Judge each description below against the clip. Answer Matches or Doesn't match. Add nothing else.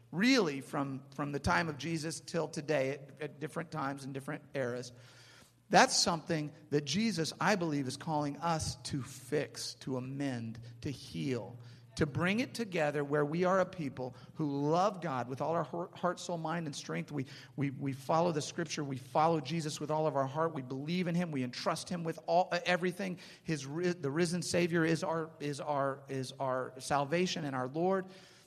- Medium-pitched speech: Matches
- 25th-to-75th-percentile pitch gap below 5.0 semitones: Matches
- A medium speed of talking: Matches